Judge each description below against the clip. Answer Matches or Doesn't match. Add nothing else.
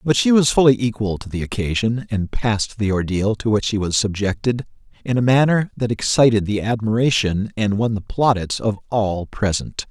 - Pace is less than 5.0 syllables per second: Doesn't match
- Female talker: Doesn't match